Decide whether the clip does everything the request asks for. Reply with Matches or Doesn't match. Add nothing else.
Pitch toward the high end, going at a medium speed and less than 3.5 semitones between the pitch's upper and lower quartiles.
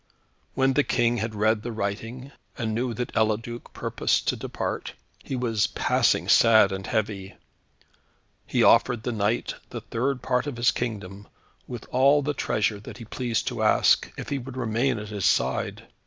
Doesn't match